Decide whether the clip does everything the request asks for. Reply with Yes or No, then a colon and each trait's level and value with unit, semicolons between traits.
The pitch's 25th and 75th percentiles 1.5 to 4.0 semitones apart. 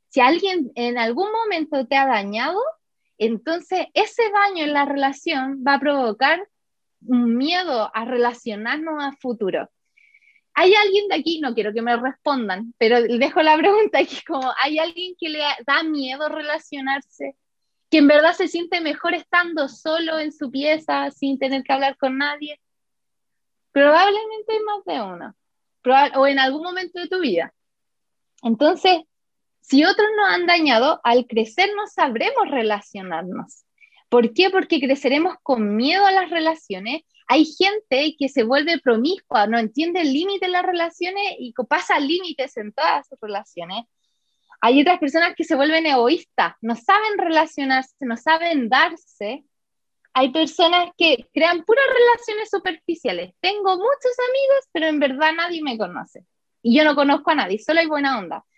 No: average, 5.2 semitones